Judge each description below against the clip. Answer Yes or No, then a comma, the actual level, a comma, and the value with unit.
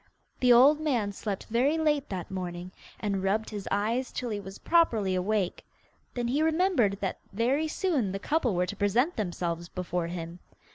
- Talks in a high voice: Yes, high, 210 Hz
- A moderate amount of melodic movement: No, wide, 5.9 semitones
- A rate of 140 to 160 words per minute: No, average, 175 wpm